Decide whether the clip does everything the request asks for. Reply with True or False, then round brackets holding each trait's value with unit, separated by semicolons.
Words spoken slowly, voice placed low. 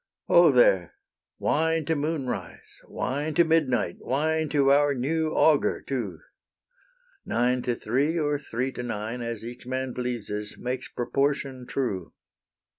True (130 wpm; 130 Hz)